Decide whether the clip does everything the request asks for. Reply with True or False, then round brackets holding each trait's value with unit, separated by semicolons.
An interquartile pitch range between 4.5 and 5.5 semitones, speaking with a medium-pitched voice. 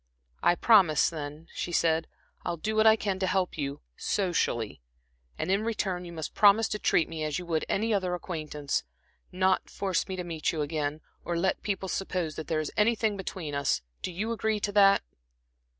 False (4.0 semitones; 180 Hz)